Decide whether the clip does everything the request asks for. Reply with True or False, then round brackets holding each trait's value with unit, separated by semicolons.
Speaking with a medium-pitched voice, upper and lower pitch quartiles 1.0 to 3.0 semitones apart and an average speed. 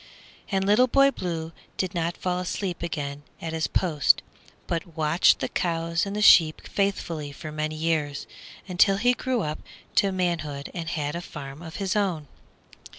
False (170 Hz; 3.7 semitones; 165 wpm)